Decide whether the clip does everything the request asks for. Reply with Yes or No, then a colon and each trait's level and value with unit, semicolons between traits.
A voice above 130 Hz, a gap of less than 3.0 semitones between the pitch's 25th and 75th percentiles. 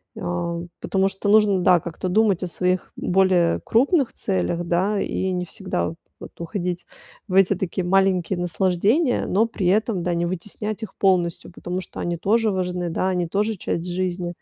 Yes: medium, 185 Hz; narrow, 2.4 semitones